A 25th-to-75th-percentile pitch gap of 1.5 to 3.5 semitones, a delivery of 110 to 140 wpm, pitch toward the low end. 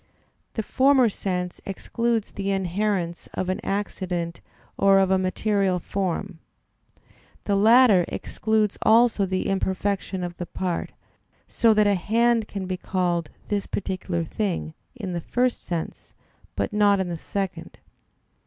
No: average, 2.8 semitones; slow, 135 wpm; high, 195 Hz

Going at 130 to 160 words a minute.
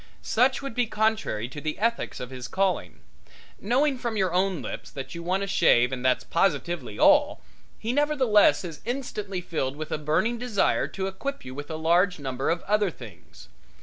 No: average, 185 wpm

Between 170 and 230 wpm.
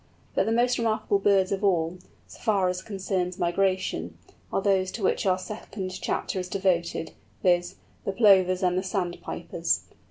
No: average, 160 wpm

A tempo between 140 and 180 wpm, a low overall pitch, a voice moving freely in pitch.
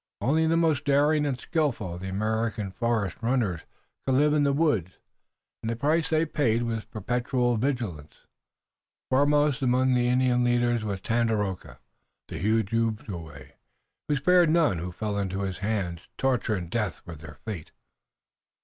Yes: average, 160 wpm; low, 115 Hz; wide, 5.8 semitones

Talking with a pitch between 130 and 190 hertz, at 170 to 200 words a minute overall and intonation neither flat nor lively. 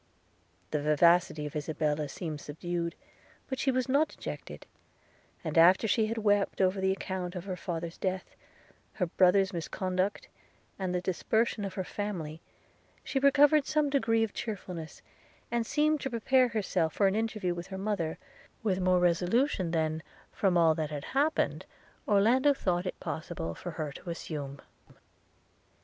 No: medium, 185 Hz; average, 155 wpm; average, 4.9 semitones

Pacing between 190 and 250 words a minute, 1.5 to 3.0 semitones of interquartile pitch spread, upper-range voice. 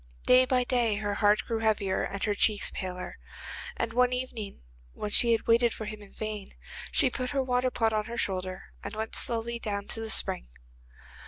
Yes: average, 195 wpm; average, 2.7 semitones; high, 220 Hz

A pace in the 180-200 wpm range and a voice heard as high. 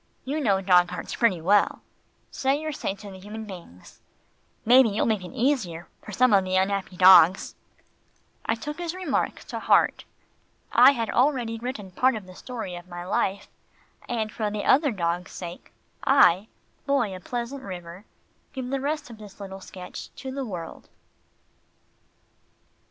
No: average, 160 wpm; high, 210 Hz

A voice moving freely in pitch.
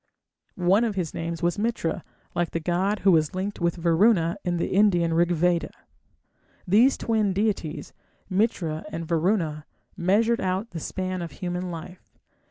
No: average, 3.2 semitones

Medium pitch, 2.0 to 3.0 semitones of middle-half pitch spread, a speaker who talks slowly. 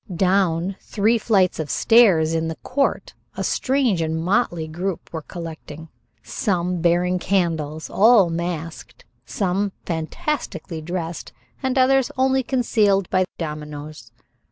No: medium, 180 Hz; average, 4.7 semitones; slow, 120 wpm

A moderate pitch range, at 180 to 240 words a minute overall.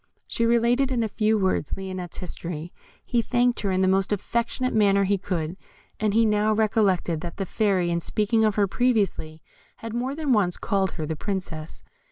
Yes: average, 3.7 semitones; average, 190 wpm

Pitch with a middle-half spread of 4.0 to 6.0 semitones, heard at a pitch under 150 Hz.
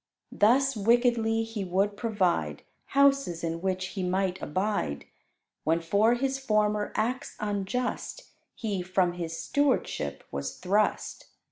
No: average, 4.6 semitones; high, 205 Hz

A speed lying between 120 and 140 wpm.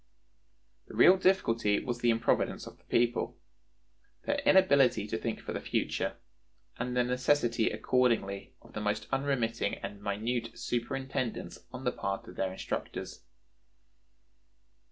Yes: slow, 135 wpm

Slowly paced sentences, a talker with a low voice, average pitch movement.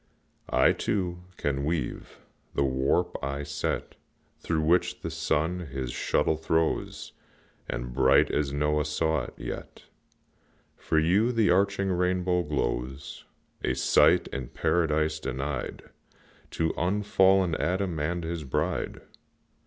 Yes: slow, 120 wpm; very low, 80 Hz; average, 4.2 semitones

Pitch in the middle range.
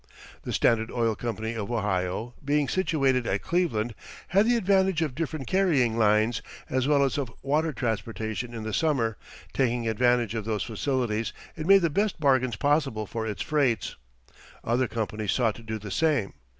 No: low, 120 Hz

